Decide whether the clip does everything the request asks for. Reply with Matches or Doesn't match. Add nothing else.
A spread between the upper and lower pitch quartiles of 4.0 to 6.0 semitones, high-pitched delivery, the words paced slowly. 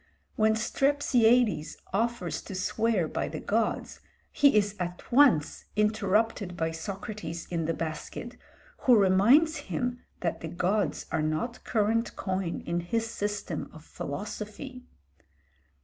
Matches